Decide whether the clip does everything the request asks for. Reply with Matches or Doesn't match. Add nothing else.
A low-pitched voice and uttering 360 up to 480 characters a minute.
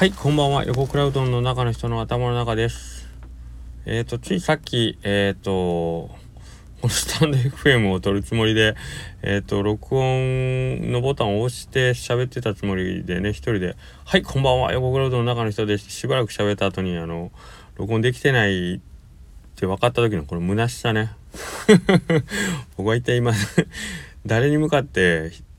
Doesn't match